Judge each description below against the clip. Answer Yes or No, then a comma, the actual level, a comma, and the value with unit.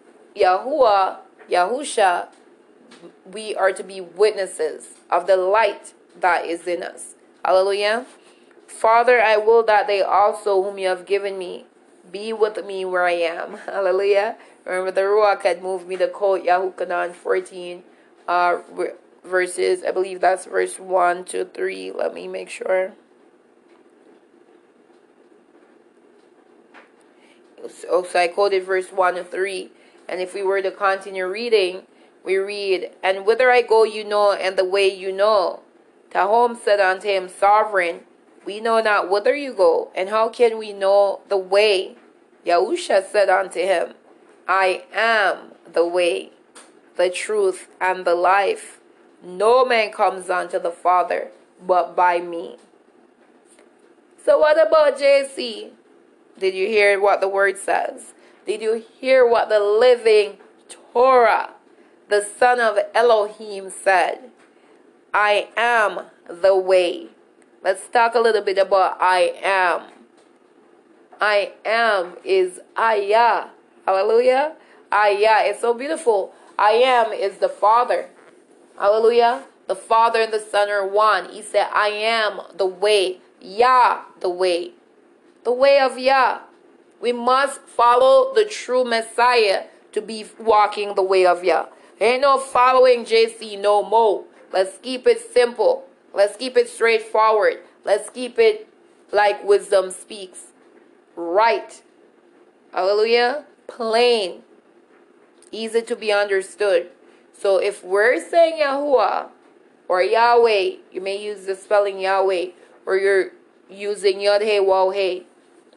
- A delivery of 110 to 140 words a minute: Yes, slow, 135 wpm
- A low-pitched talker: No, high, 215 Hz